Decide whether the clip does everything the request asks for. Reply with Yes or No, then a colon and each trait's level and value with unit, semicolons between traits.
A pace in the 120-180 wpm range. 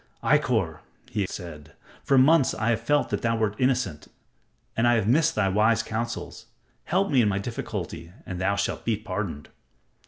Yes: average, 175 wpm